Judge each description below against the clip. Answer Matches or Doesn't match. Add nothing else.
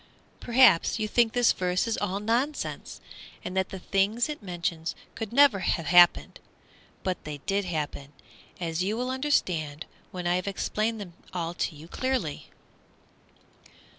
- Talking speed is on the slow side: Doesn't match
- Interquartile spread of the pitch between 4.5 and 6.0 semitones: Matches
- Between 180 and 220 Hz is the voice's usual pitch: Matches